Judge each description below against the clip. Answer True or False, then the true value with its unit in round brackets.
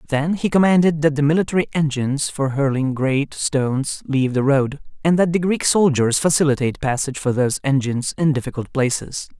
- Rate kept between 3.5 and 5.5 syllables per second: False (5.7 syllables/s)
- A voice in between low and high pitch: True (145 Hz)